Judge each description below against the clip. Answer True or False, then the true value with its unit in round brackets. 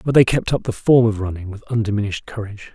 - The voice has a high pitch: False (110 Hz)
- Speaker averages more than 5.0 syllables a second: True (7.0 syllables/s)